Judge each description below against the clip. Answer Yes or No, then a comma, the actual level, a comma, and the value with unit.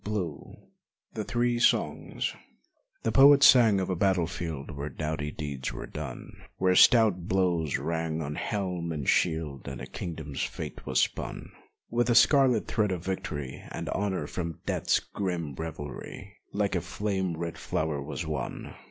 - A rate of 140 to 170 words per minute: Yes, average, 155 wpm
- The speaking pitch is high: No, very low, 85 Hz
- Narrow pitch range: No, average, 4.8 semitones